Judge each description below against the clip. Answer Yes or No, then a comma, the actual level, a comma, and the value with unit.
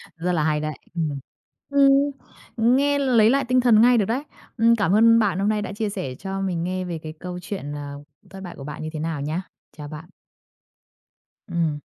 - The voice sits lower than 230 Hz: Yes, high, 190 Hz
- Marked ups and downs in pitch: Yes, wide, 6.4 semitones